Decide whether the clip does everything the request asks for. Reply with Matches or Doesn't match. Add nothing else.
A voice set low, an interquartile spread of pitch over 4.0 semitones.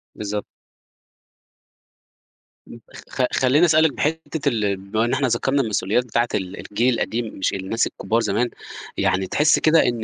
Matches